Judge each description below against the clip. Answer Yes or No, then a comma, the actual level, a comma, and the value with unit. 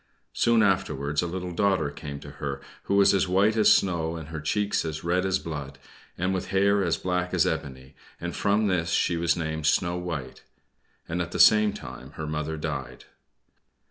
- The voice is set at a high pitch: No, very low, 85 Hz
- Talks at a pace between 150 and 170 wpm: No, average, 190 wpm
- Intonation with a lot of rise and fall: No, average, 3.5 semitones